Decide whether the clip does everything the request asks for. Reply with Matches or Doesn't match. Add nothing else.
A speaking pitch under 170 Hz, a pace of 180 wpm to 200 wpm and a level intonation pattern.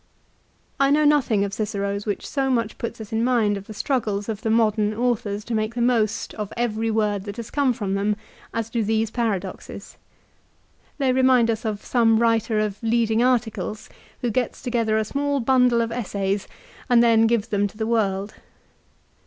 Doesn't match